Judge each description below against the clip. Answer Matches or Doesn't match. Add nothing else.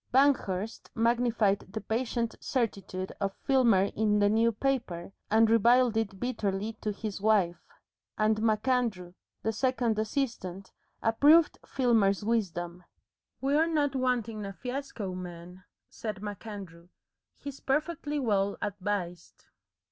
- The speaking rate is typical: Doesn't match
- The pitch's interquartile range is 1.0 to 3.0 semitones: Doesn't match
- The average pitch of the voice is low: Doesn't match